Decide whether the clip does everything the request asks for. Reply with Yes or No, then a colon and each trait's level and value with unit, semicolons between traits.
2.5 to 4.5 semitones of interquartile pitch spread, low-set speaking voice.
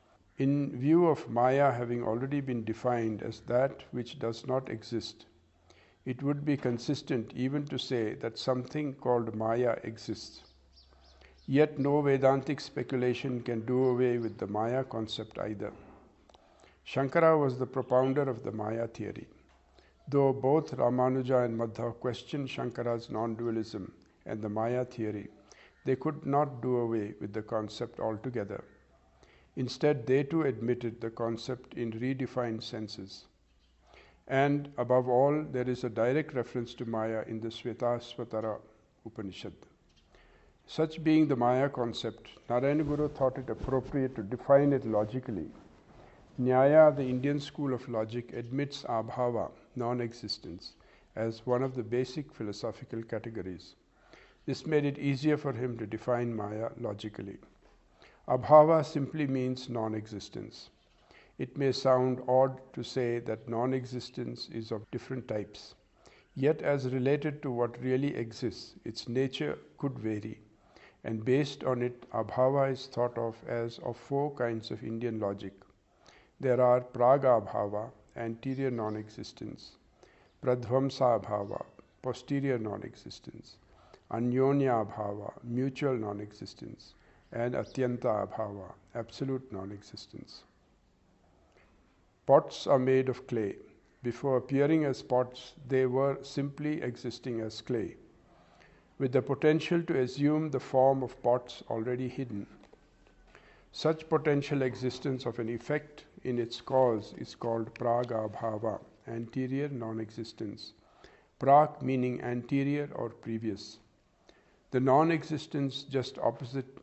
Yes: average, 3.2 semitones; low, 125 Hz